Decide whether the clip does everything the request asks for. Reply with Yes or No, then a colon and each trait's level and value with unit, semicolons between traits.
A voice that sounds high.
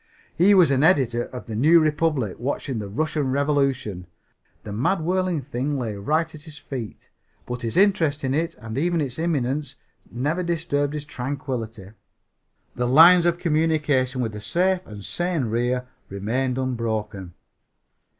No: medium, 140 Hz